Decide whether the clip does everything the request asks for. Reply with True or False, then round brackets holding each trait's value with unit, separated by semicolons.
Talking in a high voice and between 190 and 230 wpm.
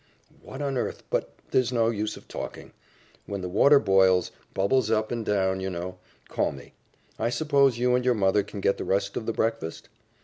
False (110 Hz; 200 wpm)